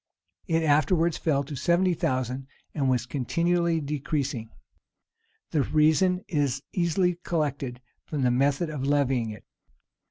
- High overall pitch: No, medium, 145 Hz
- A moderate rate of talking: No, slow, 130 wpm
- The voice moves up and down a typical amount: Yes, average, 4.1 semitones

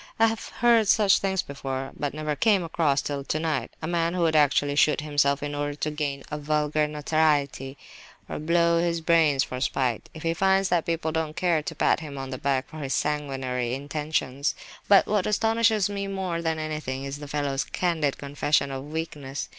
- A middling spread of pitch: Yes, average, 3.1 semitones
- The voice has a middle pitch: Yes, medium, 150 Hz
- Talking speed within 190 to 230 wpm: Yes, average, 200 wpm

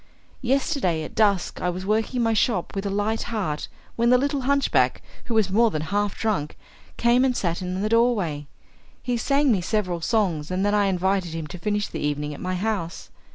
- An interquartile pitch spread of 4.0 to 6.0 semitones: Yes, average, 4.5 semitones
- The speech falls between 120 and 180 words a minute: No, fast, 205 wpm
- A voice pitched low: No, high, 205 Hz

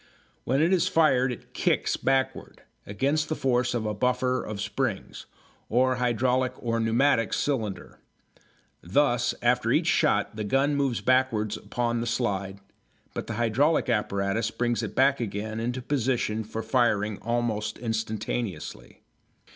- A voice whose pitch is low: Yes, low, 120 Hz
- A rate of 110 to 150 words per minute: Yes, average, 140 wpm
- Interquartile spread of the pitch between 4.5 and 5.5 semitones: No, average, 3.1 semitones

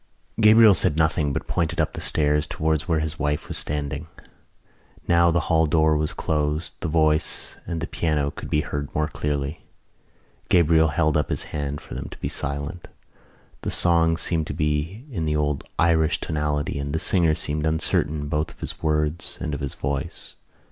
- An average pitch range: No, narrow, 1.8 semitones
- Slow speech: No, average, 185 wpm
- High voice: No, very low, 75 Hz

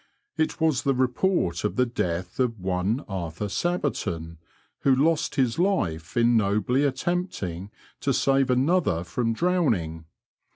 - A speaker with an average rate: No, slow, 130 wpm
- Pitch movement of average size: No, wide, 8.1 semitones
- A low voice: Yes, low, 120 Hz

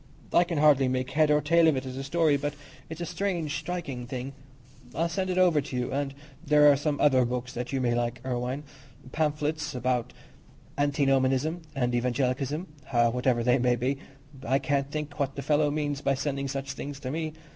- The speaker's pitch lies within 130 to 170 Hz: Yes, medium, 140 Hz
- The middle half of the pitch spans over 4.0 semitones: No, average, 2.8 semitones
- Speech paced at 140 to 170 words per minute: No, average, 200 wpm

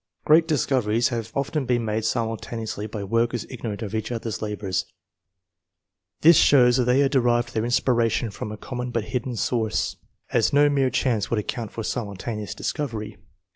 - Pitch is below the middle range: Yes, low, 115 Hz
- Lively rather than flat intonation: No, average, 2.7 semitones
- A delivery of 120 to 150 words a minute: No, average, 165 wpm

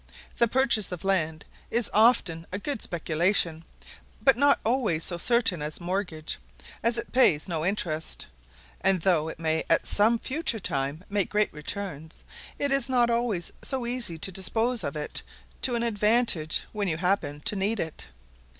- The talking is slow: No, average, 165 wpm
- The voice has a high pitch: Yes, high, 195 Hz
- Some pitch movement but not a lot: No, wide, 6.5 semitones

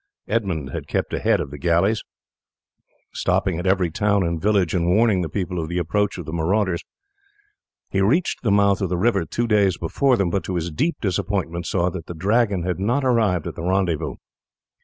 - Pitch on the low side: Yes, very low, 95 Hz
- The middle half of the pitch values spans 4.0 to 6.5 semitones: No, average, 3.2 semitones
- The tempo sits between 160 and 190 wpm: No, average, 200 wpm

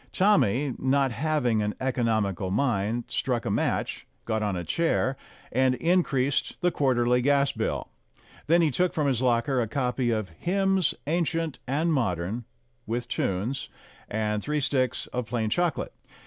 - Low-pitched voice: Yes, low, 130 Hz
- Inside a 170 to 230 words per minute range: No, average, 150 wpm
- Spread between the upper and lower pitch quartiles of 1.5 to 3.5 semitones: No, average, 4.7 semitones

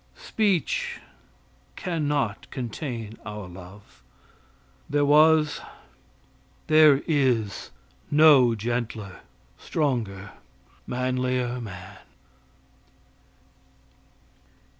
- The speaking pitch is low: Yes, low, 125 Hz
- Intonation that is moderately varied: No, wide, 5.9 semitones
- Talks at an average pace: No, slow, 60 wpm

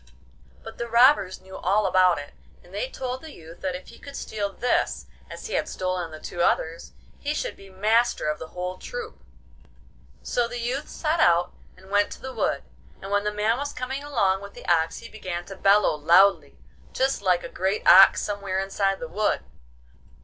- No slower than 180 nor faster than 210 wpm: Yes, average, 200 wpm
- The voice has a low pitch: No, high, 200 Hz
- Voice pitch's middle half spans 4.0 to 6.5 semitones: Yes, average, 4.7 semitones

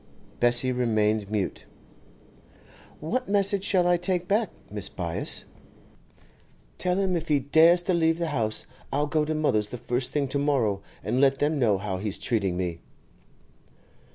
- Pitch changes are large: Yes, wide, 7.9 semitones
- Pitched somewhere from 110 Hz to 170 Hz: Yes, medium, 140 Hz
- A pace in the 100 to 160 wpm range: Yes, average, 155 wpm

